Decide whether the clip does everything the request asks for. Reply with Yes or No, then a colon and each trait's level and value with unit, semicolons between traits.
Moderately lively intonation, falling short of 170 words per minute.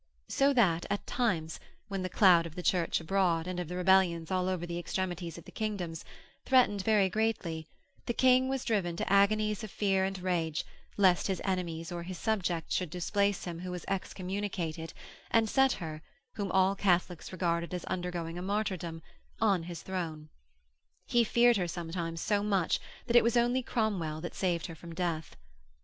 No: average, 3.2 semitones; average, 180 wpm